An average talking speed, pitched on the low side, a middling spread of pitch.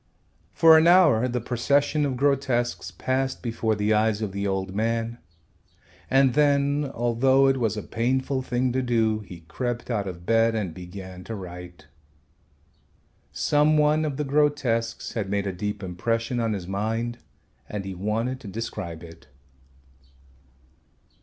Yes: average, 150 wpm; low, 115 Hz; average, 4.8 semitones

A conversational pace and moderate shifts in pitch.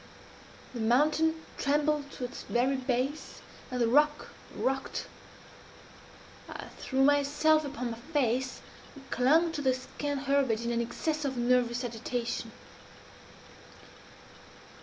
No: slow, 115 wpm; average, 3.1 semitones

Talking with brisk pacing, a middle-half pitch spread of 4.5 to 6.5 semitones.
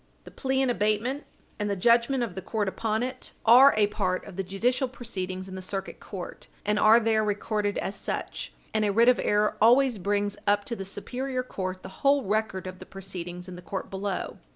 No: fast, 210 wpm; average, 3.7 semitones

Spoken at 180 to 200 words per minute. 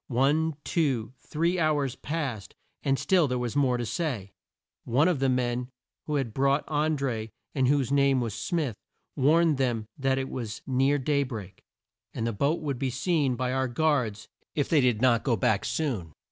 Yes: average, 185 wpm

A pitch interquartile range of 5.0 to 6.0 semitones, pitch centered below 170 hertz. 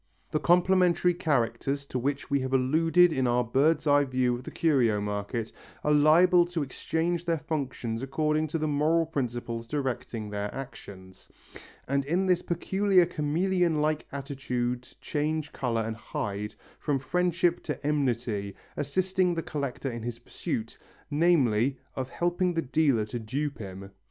Yes: average, 5.3 semitones; medium, 140 Hz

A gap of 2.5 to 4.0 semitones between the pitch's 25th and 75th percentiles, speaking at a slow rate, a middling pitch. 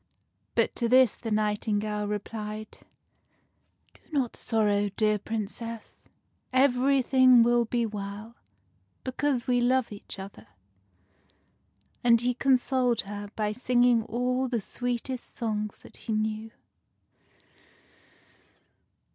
No: average, 2.8 semitones; slow, 110 wpm; high, 230 Hz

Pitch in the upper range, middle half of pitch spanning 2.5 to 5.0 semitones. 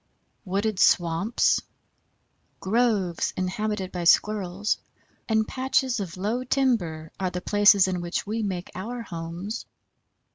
Yes: high, 200 Hz; average, 3.5 semitones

